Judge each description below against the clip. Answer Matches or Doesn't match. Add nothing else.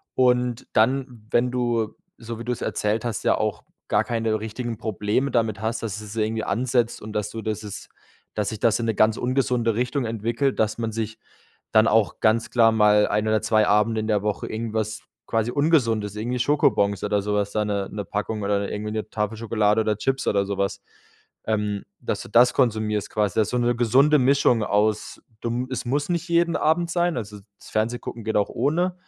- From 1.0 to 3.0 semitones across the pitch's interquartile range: Matches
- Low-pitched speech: Matches